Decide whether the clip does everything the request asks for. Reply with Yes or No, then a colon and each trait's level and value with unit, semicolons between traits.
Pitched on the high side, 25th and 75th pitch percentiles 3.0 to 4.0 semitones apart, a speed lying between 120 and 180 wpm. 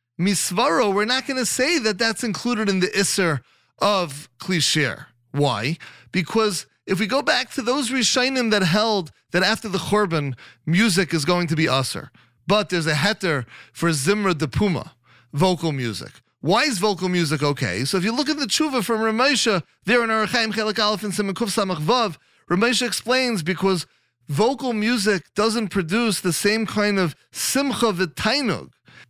No: high, 200 Hz; wide, 5.4 semitones; average, 165 wpm